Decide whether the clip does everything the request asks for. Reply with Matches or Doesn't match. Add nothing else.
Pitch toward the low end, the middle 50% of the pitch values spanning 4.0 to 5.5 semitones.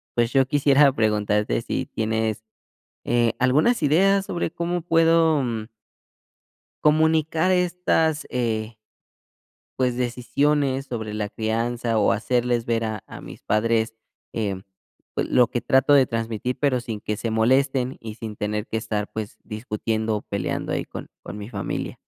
Matches